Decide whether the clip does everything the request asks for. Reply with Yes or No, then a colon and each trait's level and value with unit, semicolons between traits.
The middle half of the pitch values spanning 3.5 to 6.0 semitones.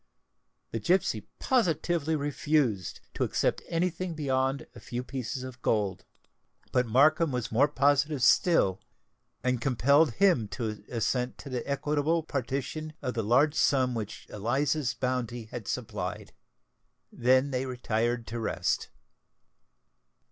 Yes: average, 4.0 semitones